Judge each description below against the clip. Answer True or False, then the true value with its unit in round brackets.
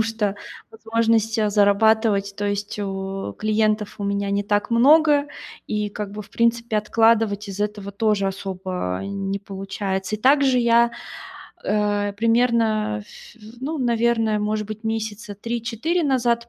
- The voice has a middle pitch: False (215 Hz)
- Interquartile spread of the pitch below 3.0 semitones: True (2.4 semitones)